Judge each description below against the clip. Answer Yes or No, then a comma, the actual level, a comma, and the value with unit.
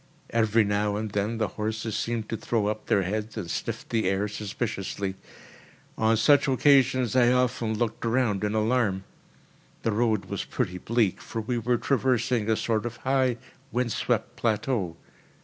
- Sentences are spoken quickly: No, average, 165 wpm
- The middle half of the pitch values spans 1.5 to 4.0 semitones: Yes, narrow, 2.4 semitones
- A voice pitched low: Yes, low, 110 Hz